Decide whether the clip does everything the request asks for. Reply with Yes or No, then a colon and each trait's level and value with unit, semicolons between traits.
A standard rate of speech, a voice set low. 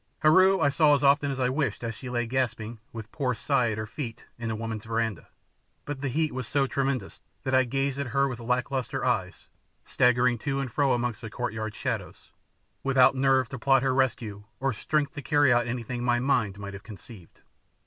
No: fast, 210 wpm; low, 125 Hz